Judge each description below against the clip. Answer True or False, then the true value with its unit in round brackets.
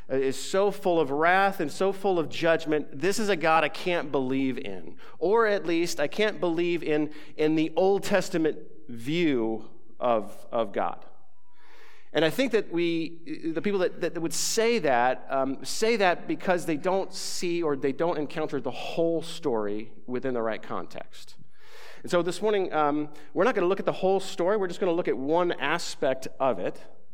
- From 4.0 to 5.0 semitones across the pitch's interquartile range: True (4.5 semitones)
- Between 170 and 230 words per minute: True (190 wpm)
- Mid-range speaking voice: True (170 Hz)